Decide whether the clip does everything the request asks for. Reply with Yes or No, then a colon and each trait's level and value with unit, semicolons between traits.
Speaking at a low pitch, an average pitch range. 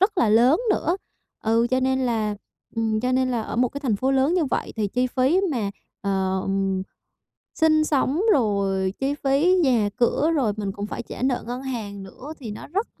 No: very high, 250 Hz; average, 4.7 semitones